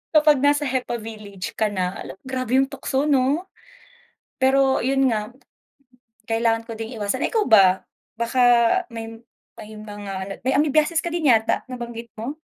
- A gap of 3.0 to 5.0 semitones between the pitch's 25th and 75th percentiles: Yes, average, 3.9 semitones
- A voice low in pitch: No, high, 240 Hz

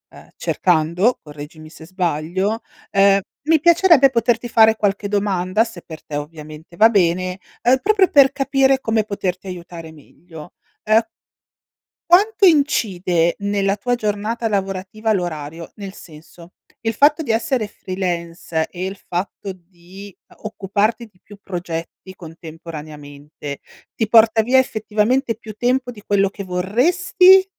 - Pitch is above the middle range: Yes, high, 200 Hz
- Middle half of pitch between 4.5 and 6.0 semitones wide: Yes, average, 4.8 semitones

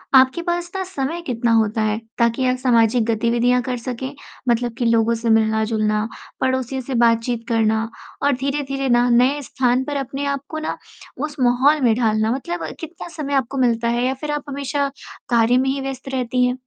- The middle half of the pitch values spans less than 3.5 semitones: Yes, average, 2.9 semitones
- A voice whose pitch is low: No, very high, 250 Hz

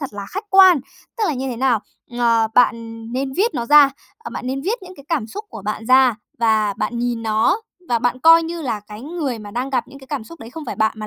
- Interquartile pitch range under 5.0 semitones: No, average, 5.3 semitones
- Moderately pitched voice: No, very high, 255 Hz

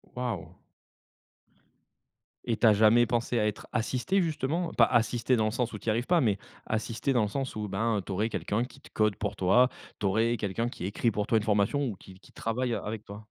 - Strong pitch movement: No, average, 2.8 semitones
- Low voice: Yes, low, 115 Hz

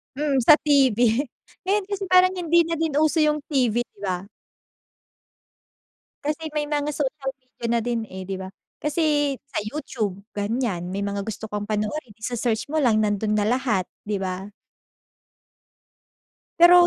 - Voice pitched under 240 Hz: No, very high, 255 Hz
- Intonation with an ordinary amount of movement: No, wide, 6.2 semitones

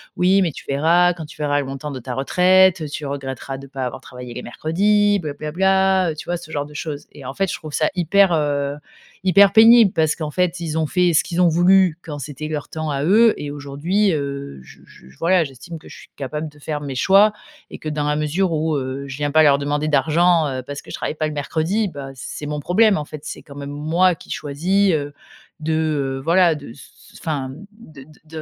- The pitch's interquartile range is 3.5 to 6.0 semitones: Yes, average, 3.8 semitones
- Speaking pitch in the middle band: Yes, medium, 155 Hz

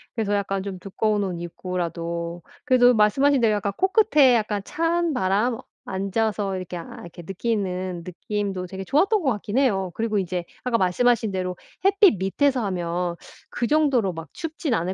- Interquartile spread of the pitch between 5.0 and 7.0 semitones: Yes, average, 5.3 semitones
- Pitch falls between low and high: No, high, 205 Hz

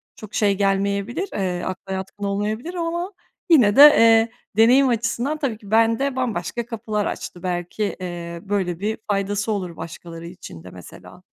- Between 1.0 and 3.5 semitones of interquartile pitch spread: No, average, 3.9 semitones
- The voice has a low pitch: No, high, 205 Hz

